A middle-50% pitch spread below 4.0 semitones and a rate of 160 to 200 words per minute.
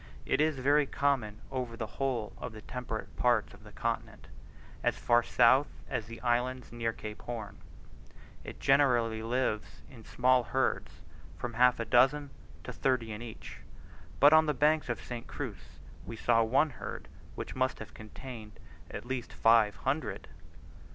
Yes: average, 2.7 semitones; average, 165 wpm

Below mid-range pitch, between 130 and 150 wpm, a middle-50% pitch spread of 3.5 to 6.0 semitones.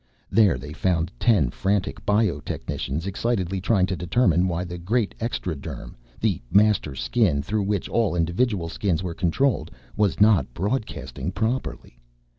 Yes: very low, 95 Hz; average, 140 wpm; average, 4.3 semitones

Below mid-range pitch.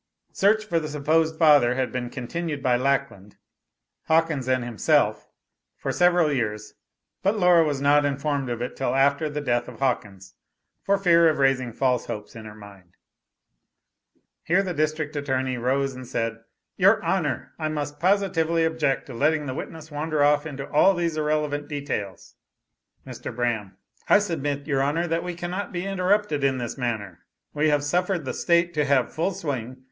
No: medium, 145 Hz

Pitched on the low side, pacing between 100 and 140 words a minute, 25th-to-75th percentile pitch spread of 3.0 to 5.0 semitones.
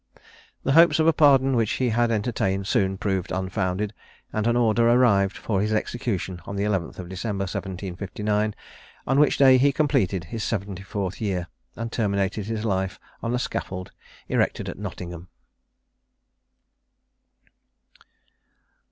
Yes: low, 105 Hz; slow, 135 wpm; average, 3.7 semitones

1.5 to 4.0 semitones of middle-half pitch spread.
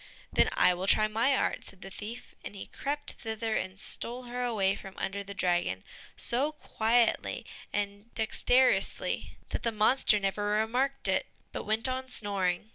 Yes: average, 3.7 semitones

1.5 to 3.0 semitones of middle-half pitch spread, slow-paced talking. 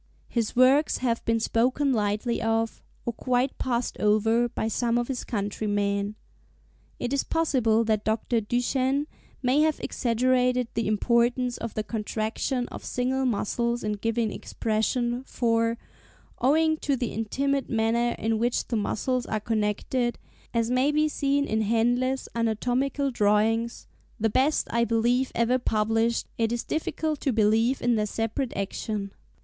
No: narrow, 2.5 semitones; average, 145 wpm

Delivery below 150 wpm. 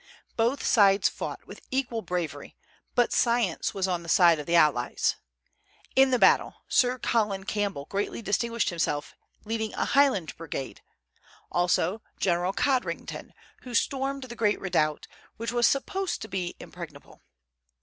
Yes: average, 140 wpm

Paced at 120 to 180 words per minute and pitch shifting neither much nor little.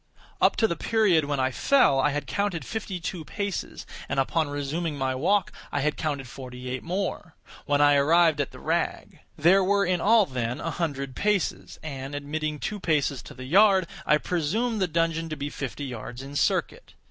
No: average, 190 wpm; average, 4.7 semitones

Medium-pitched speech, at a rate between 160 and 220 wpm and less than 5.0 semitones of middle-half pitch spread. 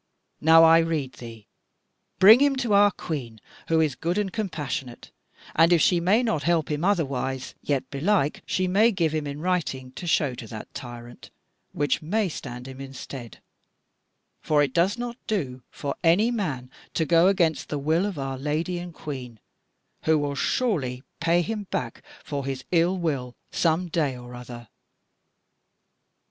No: medium, 155 Hz; average, 165 wpm; average, 5.3 semitones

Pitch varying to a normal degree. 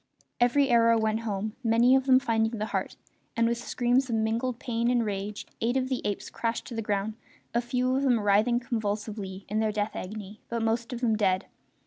No: narrow, 2.2 semitones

